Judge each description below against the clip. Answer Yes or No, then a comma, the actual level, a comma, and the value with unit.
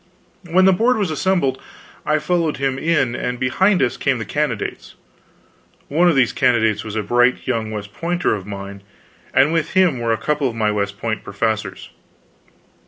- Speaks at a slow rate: No, average, 175 wpm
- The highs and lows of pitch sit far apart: Yes, wide, 7.0 semitones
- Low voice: Yes, low, 130 Hz